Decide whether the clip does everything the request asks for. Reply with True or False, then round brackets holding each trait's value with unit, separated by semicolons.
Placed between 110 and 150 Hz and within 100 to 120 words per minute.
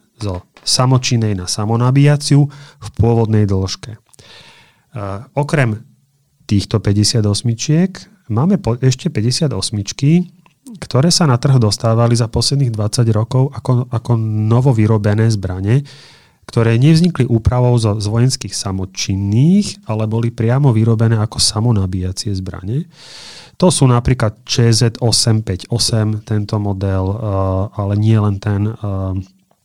True (115 Hz; 115 wpm)